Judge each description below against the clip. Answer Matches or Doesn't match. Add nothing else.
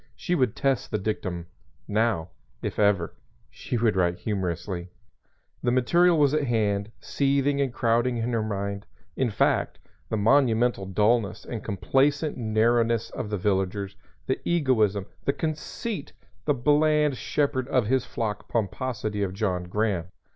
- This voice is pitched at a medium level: Doesn't match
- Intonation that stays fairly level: Doesn't match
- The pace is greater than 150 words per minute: Doesn't match